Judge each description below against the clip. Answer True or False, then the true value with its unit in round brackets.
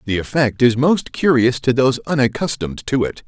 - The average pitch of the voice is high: False (130 Hz)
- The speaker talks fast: False (185 wpm)